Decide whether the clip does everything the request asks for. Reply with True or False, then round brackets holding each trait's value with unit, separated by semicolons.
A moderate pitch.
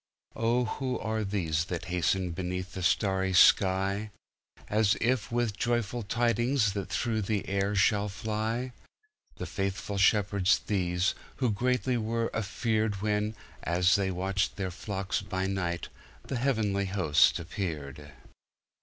False (100 Hz)